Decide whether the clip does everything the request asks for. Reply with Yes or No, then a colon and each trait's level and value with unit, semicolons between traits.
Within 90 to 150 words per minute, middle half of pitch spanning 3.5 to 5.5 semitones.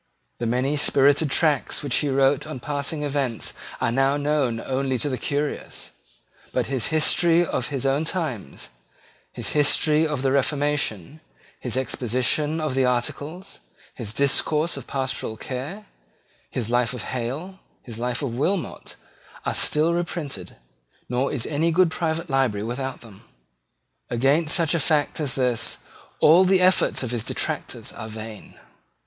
Yes: average, 145 wpm; average, 3.8 semitones